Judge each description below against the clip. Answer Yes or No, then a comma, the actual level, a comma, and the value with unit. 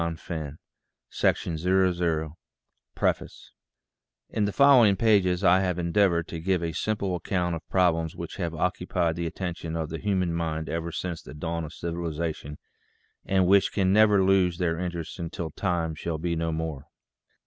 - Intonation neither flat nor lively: No, narrow, 2.3 semitones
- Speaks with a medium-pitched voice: No, very low, 85 Hz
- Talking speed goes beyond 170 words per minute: No, average, 160 wpm